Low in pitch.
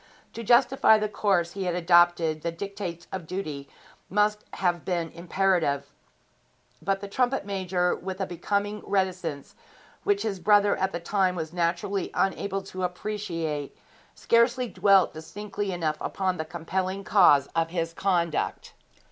No: medium, 185 Hz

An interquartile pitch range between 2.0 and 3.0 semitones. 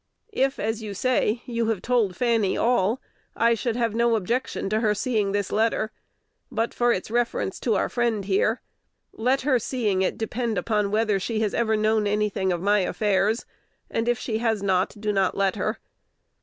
Yes: narrow, 2.5 semitones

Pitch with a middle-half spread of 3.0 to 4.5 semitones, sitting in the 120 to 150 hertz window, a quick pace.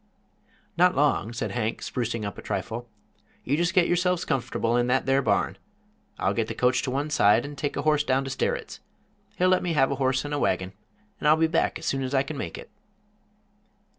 Yes: average, 4.0 semitones; low, 135 Hz; fast, 220 wpm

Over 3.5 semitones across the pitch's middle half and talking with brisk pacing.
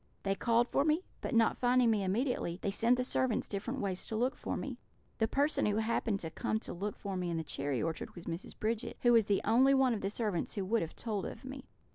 Yes: average, 4.1 semitones; fast, 250 wpm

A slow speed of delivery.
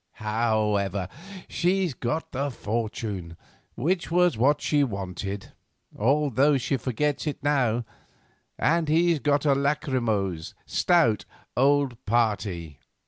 Yes: slow, 105 wpm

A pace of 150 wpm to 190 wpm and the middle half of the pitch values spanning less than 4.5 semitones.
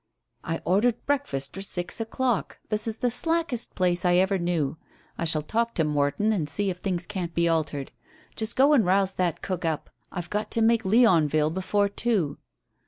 No: average, 185 wpm; average, 5.2 semitones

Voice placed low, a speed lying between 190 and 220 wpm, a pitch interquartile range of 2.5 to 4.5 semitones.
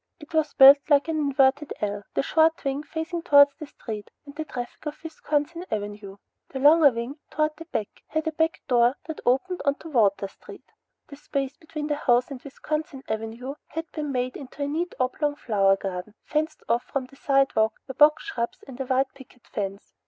No: very high, 275 Hz; average, 195 wpm; average, 4.0 semitones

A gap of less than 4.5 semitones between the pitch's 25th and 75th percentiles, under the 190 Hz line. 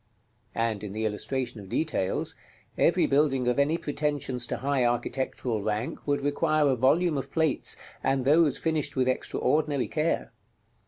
Yes: average, 3.8 semitones; low, 135 Hz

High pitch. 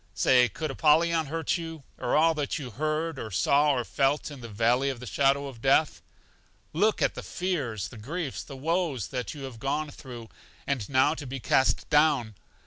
No: medium, 140 Hz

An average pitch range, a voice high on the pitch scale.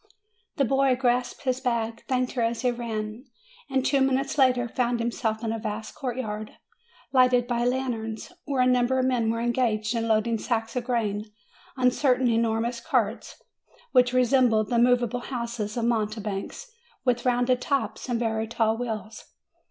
No: narrow, 2.1 semitones; high, 240 Hz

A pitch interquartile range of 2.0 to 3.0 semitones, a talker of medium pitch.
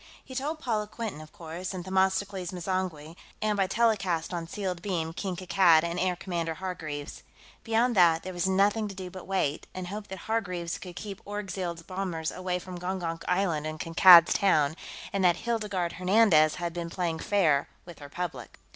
Yes: average, 2.7 semitones; medium, 180 Hz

